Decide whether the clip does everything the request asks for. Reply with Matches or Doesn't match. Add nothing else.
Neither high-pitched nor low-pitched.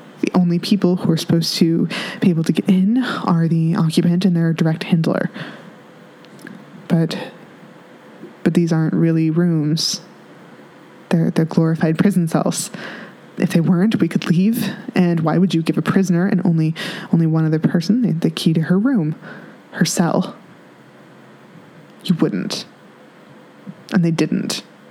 Matches